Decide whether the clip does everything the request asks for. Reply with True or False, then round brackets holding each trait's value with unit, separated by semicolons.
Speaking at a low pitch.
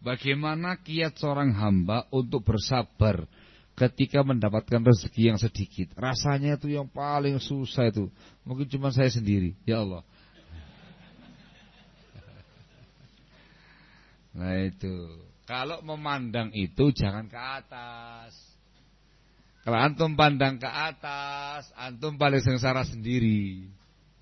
True (125 Hz)